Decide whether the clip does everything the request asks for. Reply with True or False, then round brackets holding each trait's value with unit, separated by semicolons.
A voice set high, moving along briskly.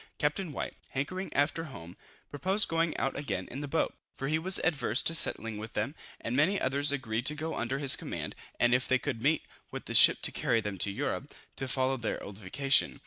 False (135 Hz; 215 wpm)